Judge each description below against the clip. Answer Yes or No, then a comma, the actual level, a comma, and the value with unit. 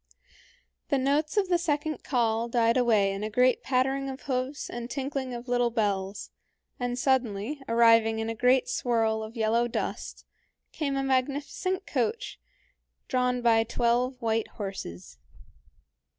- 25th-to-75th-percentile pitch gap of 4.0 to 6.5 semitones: No, average, 3.2 semitones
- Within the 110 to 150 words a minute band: Yes, average, 140 wpm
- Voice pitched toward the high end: Yes, high, 245 Hz